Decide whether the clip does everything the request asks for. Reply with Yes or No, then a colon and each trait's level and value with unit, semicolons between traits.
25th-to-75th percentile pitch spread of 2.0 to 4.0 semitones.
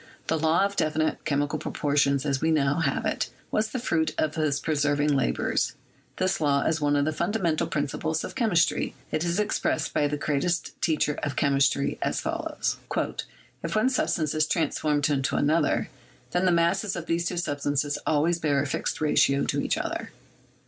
Yes: average, 2.9 semitones